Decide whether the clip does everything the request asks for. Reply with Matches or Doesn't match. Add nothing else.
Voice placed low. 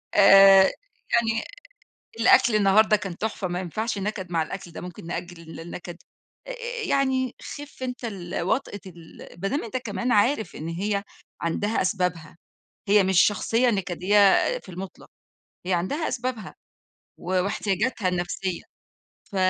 Doesn't match